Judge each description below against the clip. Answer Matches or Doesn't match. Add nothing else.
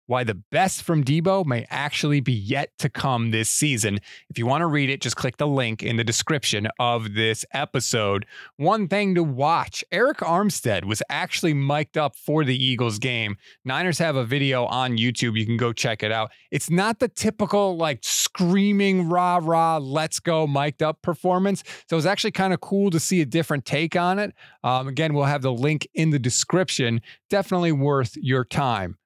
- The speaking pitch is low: Doesn't match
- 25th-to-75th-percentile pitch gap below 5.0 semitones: Doesn't match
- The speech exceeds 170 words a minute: Matches